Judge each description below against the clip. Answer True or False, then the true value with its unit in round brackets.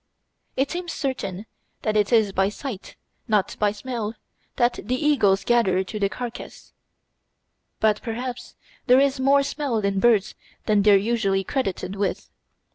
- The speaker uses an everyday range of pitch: True (4.2 semitones)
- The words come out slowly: False (150 wpm)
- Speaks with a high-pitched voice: True (220 Hz)